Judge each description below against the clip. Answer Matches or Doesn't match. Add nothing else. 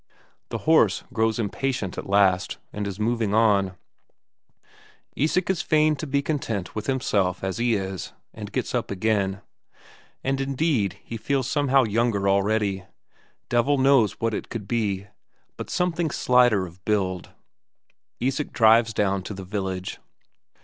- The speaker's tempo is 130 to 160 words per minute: Matches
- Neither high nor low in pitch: Doesn't match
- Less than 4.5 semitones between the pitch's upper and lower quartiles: Doesn't match